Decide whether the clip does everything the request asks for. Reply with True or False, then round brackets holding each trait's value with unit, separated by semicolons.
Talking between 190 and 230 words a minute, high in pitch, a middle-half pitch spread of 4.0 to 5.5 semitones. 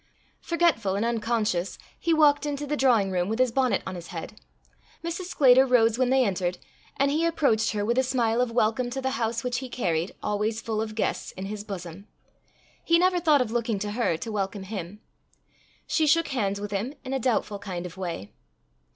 True (205 wpm; 225 Hz; 4.7 semitones)